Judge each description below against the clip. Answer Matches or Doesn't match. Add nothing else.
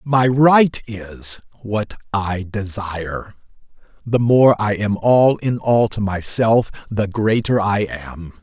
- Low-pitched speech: Matches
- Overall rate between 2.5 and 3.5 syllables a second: Matches